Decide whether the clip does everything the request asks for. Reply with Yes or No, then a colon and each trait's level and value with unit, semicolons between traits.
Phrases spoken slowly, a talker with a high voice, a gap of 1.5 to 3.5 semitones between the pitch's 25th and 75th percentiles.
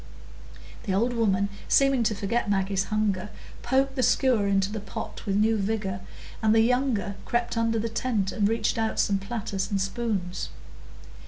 No: average, 165 wpm; high, 215 Hz; average, 2.9 semitones